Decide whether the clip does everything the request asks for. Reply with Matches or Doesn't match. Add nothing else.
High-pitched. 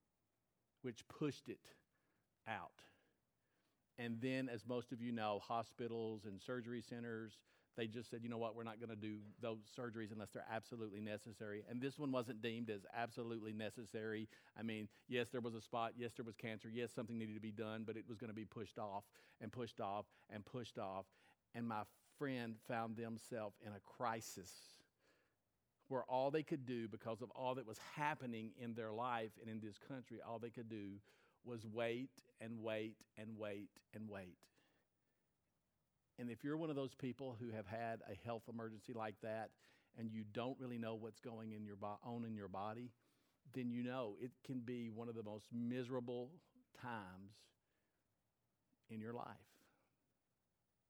Doesn't match